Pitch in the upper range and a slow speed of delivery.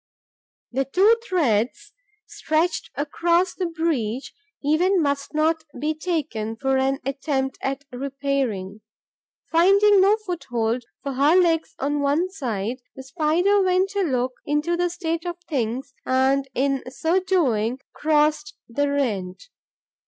Yes: very high, 290 Hz; slow, 130 wpm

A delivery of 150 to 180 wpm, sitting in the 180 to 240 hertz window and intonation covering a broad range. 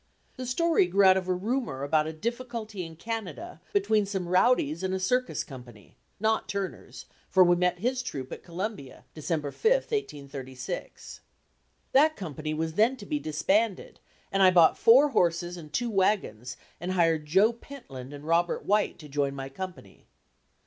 Yes: average, 165 wpm; medium, 185 Hz; wide, 6.4 semitones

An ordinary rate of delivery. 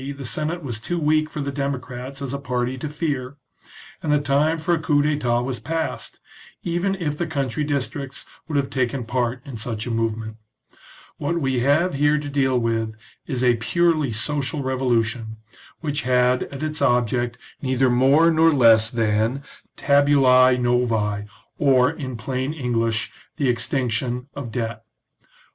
Yes: average, 160 wpm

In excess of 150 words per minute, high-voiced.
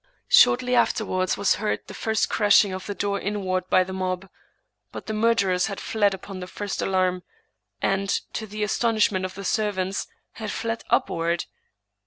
Yes: average, 170 wpm; high, 195 Hz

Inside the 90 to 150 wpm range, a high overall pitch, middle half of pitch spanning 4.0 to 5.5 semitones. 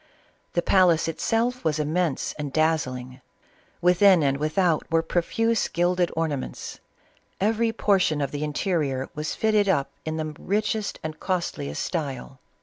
No: average, 140 wpm; medium, 165 Hz; average, 4.3 semitones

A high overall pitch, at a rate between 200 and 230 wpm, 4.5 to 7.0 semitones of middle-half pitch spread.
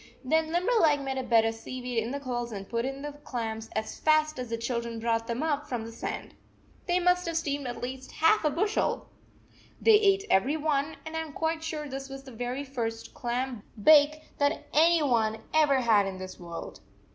Yes: very high, 270 Hz; fast, 205 wpm; average, 5.0 semitones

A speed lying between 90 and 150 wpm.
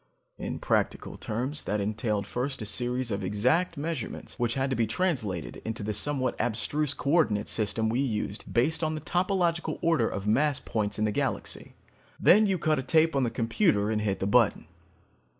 No: average, 185 wpm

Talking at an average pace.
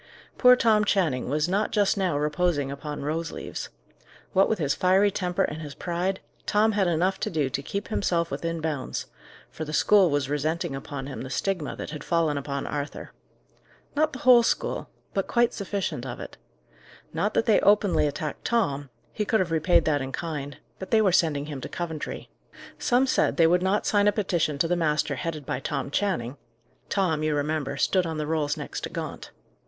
Yes: average, 195 wpm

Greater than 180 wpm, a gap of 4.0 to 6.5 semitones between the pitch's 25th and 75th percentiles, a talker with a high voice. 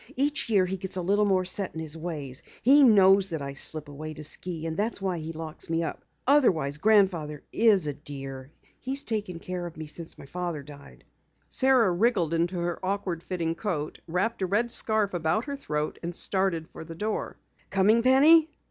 No: average, 195 wpm; average, 4.9 semitones; medium, 180 Hz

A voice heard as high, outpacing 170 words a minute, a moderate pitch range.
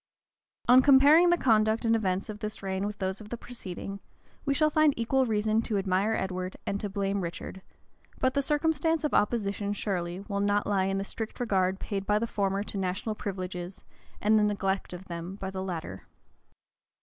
Yes: high, 205 Hz; average, 190 wpm; average, 3.0 semitones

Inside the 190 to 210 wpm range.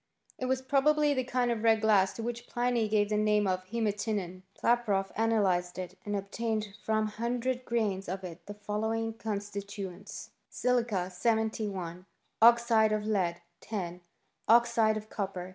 No: average, 145 wpm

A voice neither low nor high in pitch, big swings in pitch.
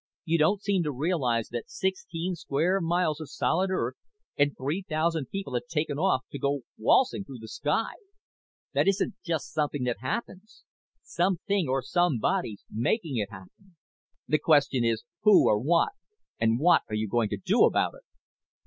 Yes: medium, 155 Hz; wide, 6.4 semitones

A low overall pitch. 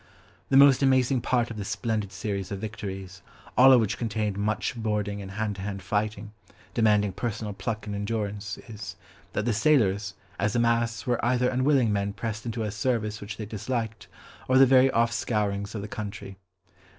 Yes: low, 110 Hz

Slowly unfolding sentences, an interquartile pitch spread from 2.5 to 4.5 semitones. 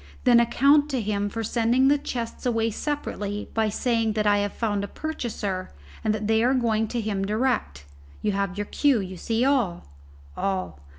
No: average, 185 wpm; average, 3.3 semitones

